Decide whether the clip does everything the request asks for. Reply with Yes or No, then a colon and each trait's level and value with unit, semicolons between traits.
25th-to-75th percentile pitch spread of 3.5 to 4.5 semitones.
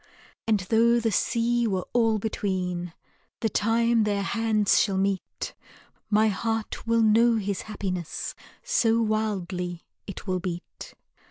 No: average, 3.1 semitones